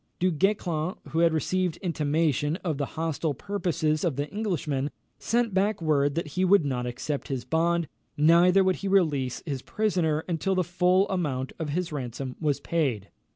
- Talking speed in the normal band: Yes, average, 170 wpm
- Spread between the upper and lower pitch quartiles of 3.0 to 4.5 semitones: Yes, average, 4.1 semitones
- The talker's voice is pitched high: No, medium, 160 Hz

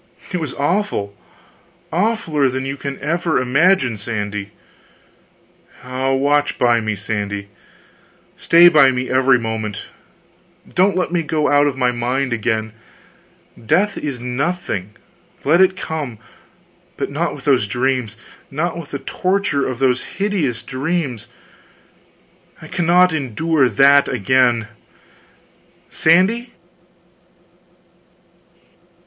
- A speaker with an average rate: No, slow, 110 wpm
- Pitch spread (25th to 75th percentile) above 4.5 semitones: Yes, wide, 5.5 semitones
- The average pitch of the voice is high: No, low, 135 Hz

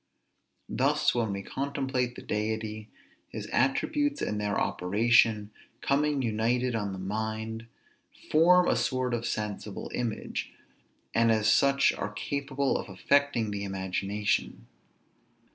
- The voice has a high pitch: No, low, 115 Hz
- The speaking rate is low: Yes, slow, 120 wpm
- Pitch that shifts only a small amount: No, average, 4.2 semitones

